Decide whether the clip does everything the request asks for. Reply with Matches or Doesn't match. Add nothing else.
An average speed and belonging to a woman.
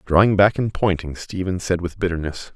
Doesn't match